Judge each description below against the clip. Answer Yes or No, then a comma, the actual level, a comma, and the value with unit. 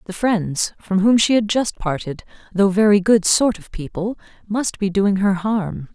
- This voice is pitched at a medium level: No, high, 200 Hz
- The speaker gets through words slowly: No, average, 190 wpm